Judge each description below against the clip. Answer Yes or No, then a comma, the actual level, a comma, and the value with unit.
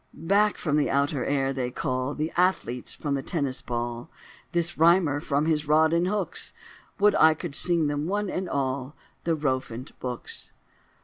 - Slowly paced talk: No, average, 170 wpm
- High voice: No, medium, 150 Hz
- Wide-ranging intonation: No, average, 4.1 semitones